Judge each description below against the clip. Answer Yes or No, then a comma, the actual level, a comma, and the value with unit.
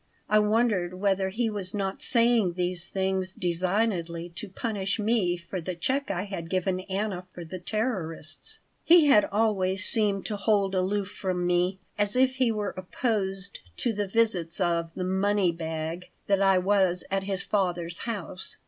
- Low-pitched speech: No, high, 190 Hz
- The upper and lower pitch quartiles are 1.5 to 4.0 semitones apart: Yes, average, 2.8 semitones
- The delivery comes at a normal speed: Yes, average, 165 wpm